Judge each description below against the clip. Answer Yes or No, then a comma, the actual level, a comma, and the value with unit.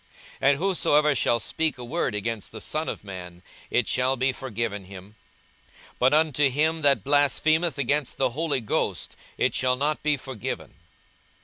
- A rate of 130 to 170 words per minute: Yes, average, 165 wpm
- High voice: No, low, 135 Hz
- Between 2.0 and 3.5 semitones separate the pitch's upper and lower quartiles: No, average, 4.5 semitones